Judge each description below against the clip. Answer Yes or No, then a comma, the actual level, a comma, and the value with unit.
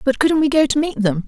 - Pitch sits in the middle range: No, very high, 270 Hz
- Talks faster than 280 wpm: Yes, fast, 330 wpm